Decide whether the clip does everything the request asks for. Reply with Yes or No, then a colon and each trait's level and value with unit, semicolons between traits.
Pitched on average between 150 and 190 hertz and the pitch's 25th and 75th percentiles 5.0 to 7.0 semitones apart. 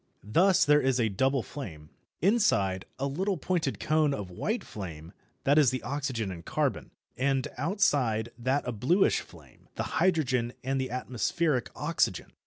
No: low, 135 Hz; wide, 5.4 semitones